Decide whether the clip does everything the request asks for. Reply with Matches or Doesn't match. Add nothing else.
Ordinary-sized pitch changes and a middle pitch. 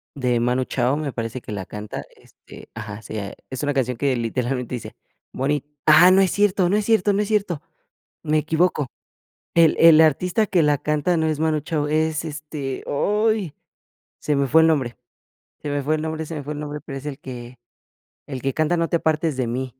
Matches